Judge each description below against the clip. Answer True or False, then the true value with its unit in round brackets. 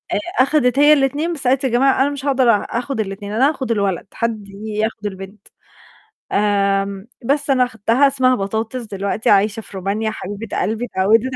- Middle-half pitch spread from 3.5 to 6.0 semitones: True (4.5 semitones)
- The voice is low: False (225 Hz)